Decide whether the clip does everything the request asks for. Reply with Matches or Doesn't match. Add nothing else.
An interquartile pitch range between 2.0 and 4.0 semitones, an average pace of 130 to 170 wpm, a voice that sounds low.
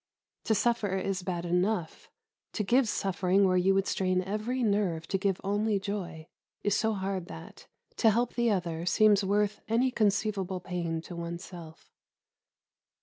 Doesn't match